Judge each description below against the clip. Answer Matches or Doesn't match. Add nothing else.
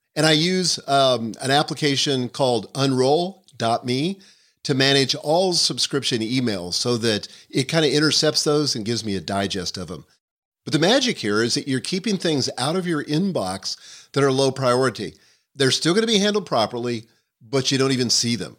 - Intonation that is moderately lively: Matches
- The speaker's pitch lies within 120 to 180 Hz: Matches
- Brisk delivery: Doesn't match